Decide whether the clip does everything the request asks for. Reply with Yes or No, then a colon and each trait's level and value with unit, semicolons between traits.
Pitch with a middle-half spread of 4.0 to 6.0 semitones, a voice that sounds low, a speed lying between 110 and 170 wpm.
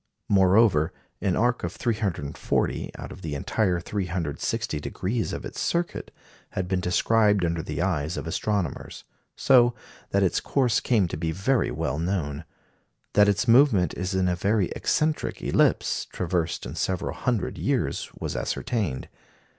Yes: average, 4.6 semitones; very low, 95 Hz; average, 145 wpm